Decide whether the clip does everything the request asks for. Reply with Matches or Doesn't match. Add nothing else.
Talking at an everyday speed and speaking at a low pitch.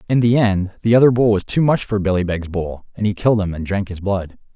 Doesn't match